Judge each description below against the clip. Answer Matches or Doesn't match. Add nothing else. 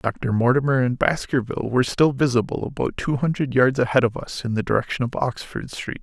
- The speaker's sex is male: Matches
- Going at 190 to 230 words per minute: Matches